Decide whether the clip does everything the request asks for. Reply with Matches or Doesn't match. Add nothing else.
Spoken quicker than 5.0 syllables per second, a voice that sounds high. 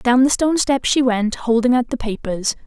Matches